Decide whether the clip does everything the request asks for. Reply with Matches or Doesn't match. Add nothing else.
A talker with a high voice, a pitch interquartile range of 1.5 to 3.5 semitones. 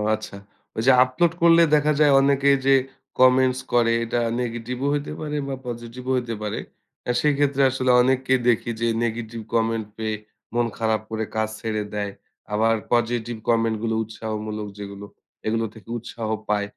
Doesn't match